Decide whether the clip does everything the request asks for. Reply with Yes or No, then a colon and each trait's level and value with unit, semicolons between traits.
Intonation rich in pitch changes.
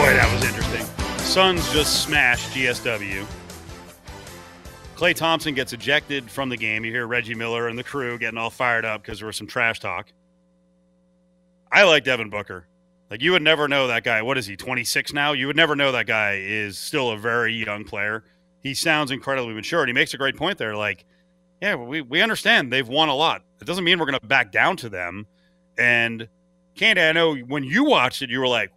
Yes: wide, 5.8 semitones